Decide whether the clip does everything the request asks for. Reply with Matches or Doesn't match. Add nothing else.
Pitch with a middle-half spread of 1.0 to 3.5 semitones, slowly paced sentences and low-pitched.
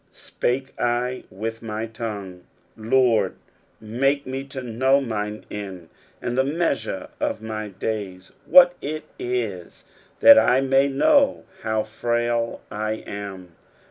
Doesn't match